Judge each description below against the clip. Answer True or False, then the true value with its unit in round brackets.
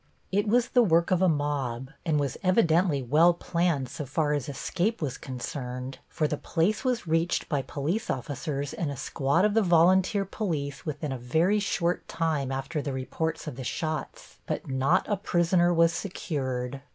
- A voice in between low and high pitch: True (160 Hz)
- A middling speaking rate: True (175 wpm)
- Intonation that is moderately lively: True (4.3 semitones)